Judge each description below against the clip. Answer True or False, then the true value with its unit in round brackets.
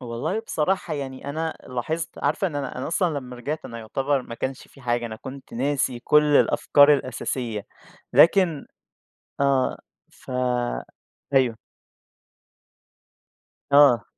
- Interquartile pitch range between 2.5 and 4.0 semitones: True (3.3 semitones)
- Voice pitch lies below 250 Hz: True (135 Hz)